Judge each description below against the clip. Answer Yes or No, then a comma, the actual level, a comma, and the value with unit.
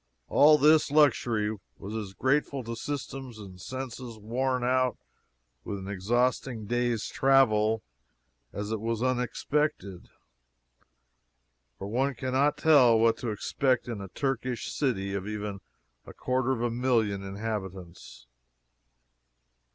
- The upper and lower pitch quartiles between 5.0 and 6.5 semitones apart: No, average, 3.9 semitones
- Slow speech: Yes, slow, 125 wpm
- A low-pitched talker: Yes, low, 120 Hz